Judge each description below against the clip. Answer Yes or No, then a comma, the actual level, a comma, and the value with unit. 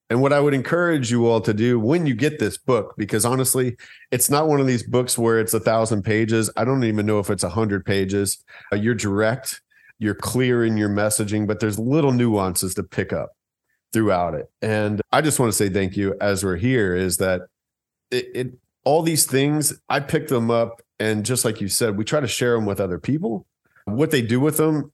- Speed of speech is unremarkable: No, fast, 220 wpm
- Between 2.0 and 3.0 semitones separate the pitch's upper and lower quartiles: No, average, 3.8 semitones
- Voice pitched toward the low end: Yes, low, 115 Hz